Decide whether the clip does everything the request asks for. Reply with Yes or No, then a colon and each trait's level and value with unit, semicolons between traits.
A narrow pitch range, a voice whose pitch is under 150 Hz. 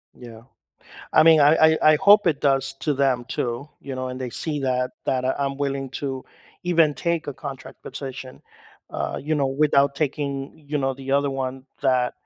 Yes: narrow, 2.0 semitones; low, 135 Hz